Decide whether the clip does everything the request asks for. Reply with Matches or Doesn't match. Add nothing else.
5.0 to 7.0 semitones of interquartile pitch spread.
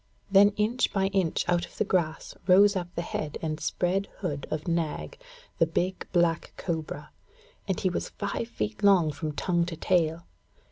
Doesn't match